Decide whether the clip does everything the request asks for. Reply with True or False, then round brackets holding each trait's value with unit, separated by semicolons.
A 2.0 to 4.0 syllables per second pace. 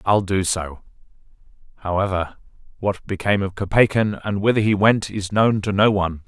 False (5.3 syllables/s)